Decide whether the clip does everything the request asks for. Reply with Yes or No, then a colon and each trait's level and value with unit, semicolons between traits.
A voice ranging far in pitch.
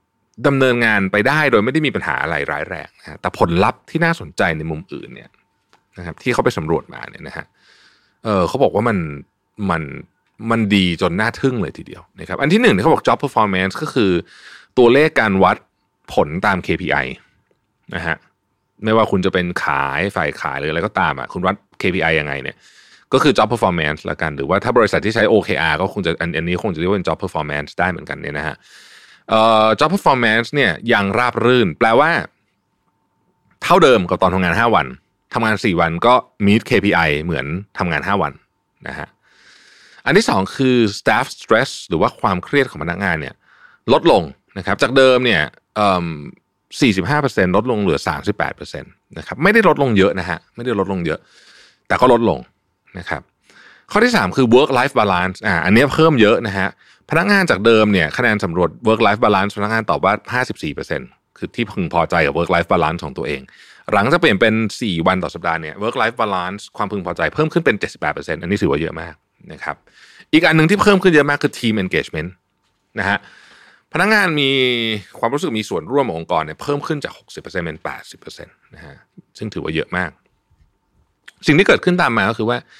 Yes: wide, 5.8 semitones